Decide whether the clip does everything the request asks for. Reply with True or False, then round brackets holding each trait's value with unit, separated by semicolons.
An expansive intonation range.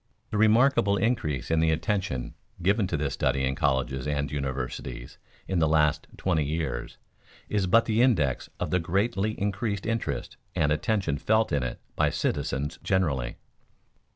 True (6.7 semitones)